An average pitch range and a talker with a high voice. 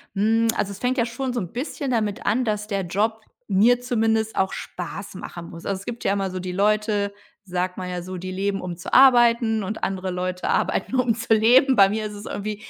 Yes: average, 3.4 semitones; high, 210 Hz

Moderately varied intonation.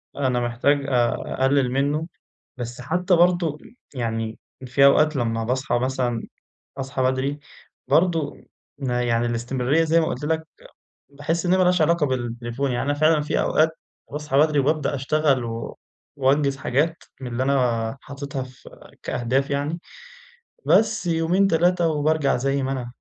Yes: average, 3.8 semitones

